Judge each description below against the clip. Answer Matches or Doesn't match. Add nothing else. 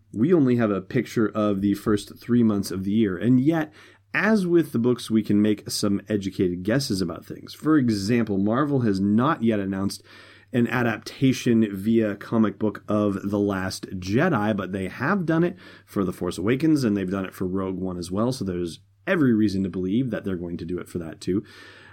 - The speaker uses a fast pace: Matches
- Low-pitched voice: Matches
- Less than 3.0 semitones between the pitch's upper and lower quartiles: Doesn't match